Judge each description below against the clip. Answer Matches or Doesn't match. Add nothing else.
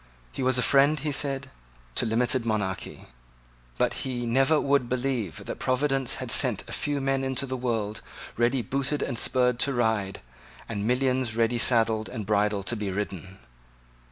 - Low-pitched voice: Matches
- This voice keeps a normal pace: Matches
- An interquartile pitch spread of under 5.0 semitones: Matches